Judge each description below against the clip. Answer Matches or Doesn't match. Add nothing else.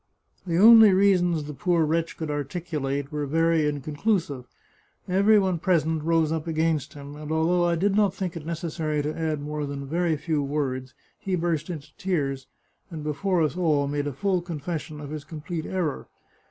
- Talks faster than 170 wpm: Matches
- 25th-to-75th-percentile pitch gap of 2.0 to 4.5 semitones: Matches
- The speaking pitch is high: Doesn't match